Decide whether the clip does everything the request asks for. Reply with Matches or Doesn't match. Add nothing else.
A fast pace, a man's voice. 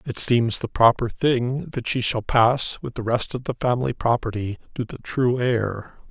Doesn't match